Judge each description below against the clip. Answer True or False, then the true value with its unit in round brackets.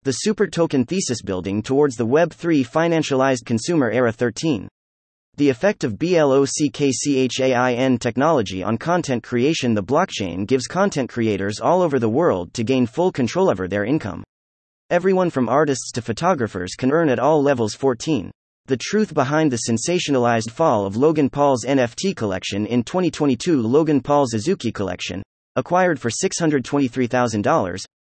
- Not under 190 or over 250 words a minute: False (145 wpm)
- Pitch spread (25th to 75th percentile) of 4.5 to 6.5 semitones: True (5.2 semitones)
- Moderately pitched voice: False (130 Hz)